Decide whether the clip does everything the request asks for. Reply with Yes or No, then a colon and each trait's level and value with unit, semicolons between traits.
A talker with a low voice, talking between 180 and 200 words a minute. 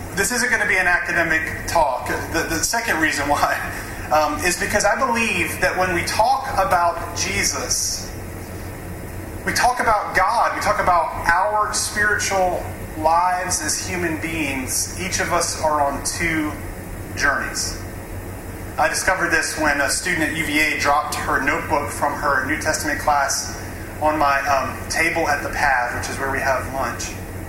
No: low, 110 Hz; average, 160 wpm